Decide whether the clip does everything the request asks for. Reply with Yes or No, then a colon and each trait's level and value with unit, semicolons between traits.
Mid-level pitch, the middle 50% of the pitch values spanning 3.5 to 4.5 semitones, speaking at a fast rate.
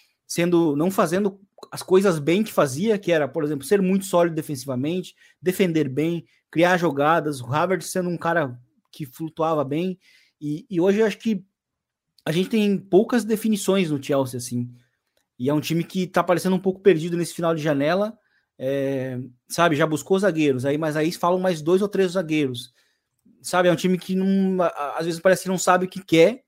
Yes: medium, 170 Hz; average, 3.8 semitones; fast, 195 wpm